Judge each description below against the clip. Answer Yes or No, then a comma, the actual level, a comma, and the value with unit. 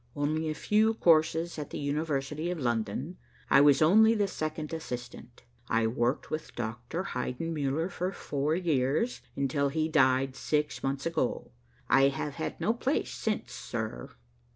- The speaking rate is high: No, average, 150 wpm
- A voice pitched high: No, medium, 150 Hz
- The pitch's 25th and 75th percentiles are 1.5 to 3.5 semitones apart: No, average, 3.9 semitones